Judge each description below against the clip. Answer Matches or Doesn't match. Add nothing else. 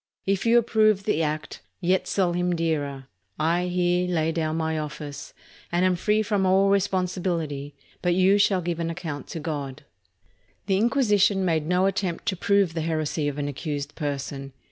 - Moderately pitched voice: Matches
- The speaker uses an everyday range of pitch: Matches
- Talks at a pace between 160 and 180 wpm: Matches